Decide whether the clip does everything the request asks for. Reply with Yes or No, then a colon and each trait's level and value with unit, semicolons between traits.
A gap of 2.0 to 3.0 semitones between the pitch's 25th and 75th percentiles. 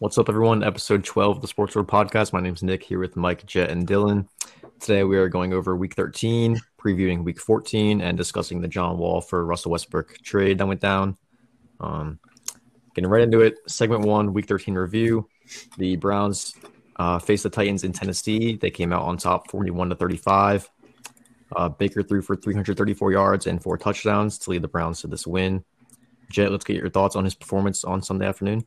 Yes: narrow, 2.4 semitones